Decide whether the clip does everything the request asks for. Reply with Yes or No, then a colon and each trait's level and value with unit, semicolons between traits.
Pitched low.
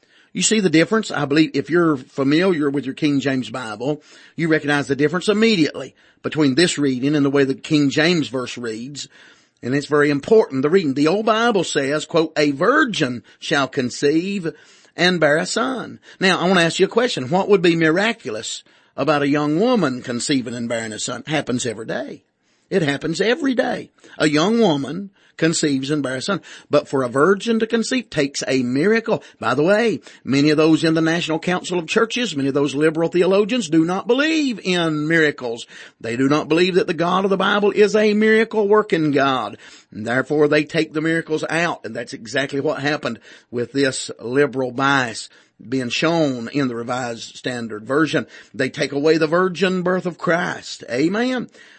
No: medium, 155 Hz